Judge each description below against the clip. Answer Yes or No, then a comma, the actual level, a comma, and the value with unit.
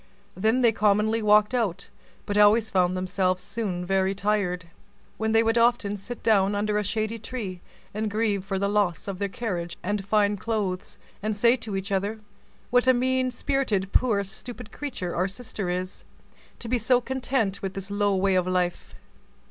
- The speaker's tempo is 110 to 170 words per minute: No, average, 180 wpm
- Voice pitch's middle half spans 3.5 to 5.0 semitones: No, average, 2.9 semitones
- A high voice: Yes, high, 205 Hz